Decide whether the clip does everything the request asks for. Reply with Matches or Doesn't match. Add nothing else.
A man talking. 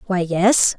Doesn't match